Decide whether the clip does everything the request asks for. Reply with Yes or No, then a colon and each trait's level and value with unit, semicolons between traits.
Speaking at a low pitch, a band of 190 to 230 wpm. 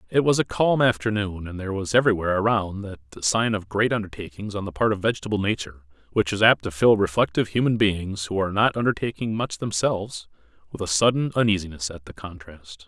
Yes: low, 100 Hz; average, 195 wpm